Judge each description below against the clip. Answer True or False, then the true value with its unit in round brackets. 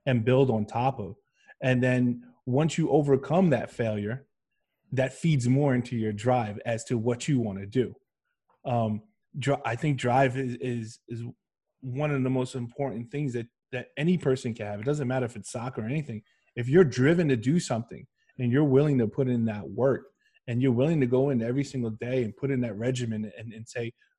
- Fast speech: True (210 wpm)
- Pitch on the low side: True (125 Hz)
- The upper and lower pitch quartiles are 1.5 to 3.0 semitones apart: True (2.6 semitones)